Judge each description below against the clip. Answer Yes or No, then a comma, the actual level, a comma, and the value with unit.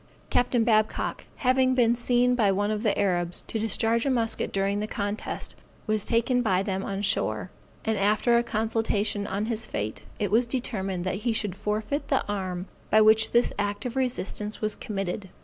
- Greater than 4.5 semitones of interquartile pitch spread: No, average, 2.8 semitones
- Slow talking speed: No, average, 185 wpm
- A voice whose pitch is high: Yes, high, 215 Hz